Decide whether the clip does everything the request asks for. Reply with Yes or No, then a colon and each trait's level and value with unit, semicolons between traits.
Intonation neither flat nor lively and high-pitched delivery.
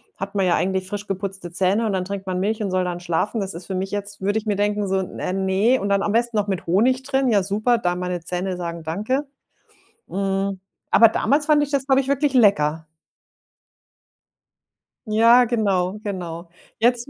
Yes: average, 3.6 semitones; high, 200 Hz